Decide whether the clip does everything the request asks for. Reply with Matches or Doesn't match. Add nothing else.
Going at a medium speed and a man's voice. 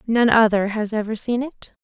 Doesn't match